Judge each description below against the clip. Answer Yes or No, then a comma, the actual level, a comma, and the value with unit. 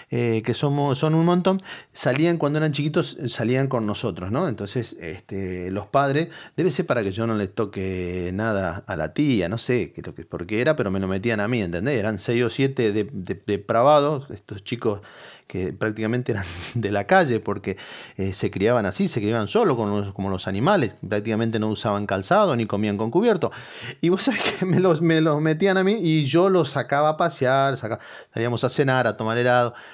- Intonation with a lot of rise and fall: Yes, wide, 6.5 semitones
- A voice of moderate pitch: No, low, 120 Hz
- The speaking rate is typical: No, fast, 210 wpm